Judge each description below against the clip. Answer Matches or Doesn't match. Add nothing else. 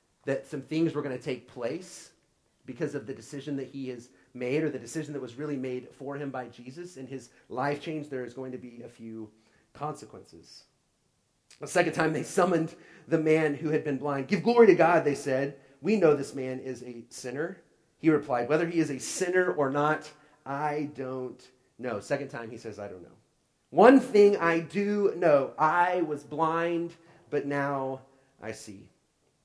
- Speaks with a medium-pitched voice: Matches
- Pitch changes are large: Doesn't match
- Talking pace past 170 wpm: Matches